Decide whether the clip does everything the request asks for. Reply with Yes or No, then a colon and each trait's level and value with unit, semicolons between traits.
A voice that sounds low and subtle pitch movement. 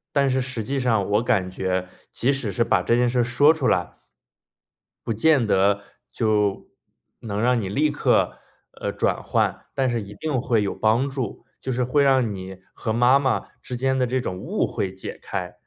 No: low, 120 Hz; average, 4.4 semitones